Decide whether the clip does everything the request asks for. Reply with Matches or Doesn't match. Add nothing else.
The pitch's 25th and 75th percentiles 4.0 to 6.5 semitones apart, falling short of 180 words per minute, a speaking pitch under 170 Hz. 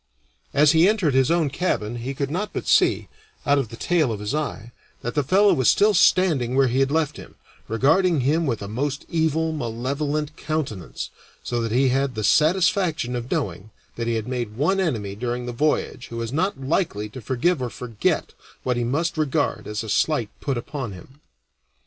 Doesn't match